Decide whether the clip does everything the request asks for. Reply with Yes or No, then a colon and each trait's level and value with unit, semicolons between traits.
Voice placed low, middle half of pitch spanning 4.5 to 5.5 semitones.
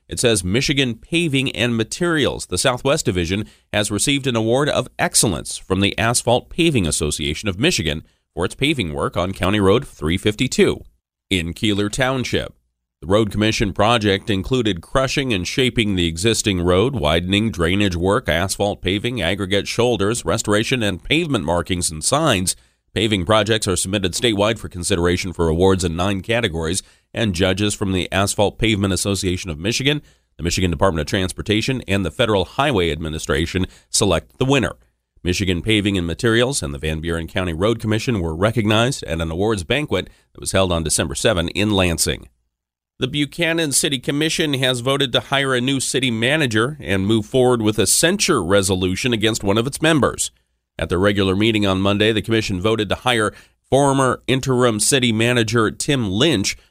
Yes: low, 105 Hz; average, 5.1 semitones